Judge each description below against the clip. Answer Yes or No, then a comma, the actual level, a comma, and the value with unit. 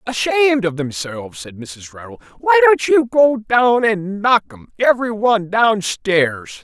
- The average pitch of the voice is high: Yes, high, 205 Hz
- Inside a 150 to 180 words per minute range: Yes, average, 155 wpm